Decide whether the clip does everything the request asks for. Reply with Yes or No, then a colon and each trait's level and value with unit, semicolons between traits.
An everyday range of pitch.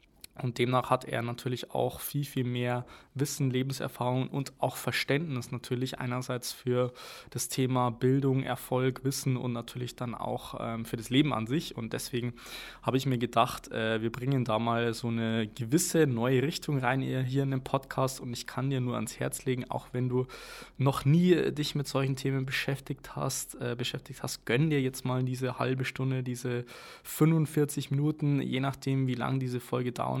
No: narrow, 1.8 semitones